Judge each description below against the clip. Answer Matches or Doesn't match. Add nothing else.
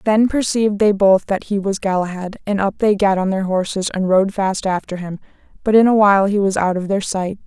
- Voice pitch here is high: Matches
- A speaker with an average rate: Doesn't match